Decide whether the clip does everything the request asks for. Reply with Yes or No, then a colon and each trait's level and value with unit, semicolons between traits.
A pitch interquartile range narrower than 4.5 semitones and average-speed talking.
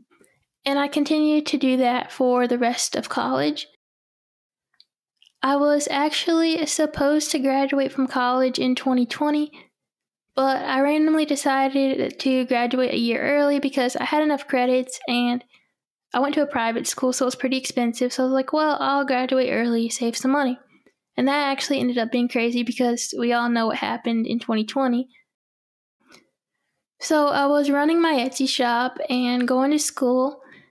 Yes: narrow, 2.6 semitones; average, 165 wpm